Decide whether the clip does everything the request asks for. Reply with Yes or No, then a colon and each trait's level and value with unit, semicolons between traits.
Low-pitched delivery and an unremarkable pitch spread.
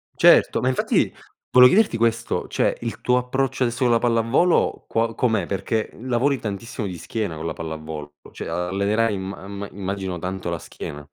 Yes: low, 110 Hz; average, 4.6 semitones